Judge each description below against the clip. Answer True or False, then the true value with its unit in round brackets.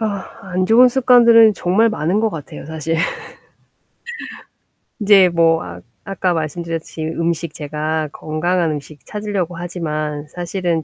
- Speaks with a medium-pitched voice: True (170 Hz)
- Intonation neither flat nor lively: True (4.0 semitones)